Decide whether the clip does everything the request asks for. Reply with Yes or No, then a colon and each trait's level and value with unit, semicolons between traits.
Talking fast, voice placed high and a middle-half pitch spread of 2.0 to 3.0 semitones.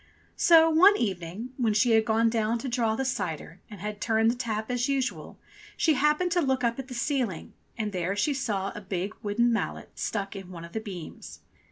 No: fast, 210 wpm; high, 225 Hz; average, 4.3 semitones